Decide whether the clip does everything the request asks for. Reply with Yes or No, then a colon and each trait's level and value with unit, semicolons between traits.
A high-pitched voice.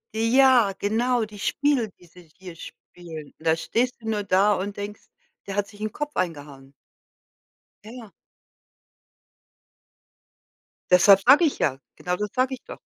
Yes: high, 205 Hz